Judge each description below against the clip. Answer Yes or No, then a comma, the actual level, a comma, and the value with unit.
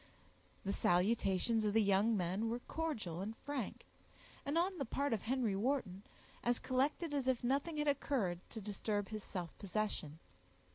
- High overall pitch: Yes, high, 225 Hz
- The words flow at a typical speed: Yes, average, 160 wpm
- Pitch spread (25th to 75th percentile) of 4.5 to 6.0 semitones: Yes, wide, 5.6 semitones